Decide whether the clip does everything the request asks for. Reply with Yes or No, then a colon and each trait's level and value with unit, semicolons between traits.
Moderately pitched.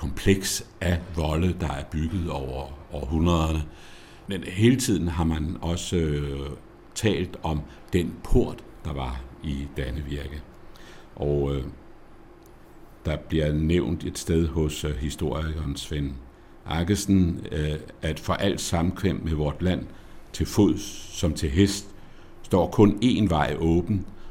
No: very low, 80 Hz